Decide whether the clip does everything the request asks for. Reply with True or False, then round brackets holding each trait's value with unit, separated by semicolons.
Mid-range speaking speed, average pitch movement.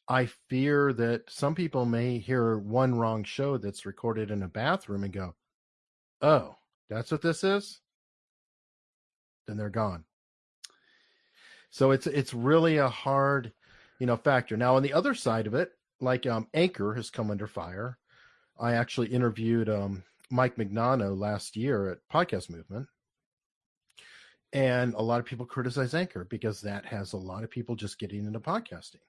True (160 wpm; 3.9 semitones)